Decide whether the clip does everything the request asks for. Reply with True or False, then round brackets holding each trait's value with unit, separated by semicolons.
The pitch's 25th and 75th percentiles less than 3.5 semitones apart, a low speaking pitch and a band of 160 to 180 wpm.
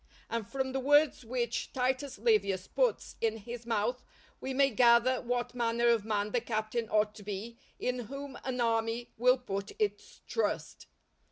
False (2.5 semitones; 240 Hz; 165 wpm)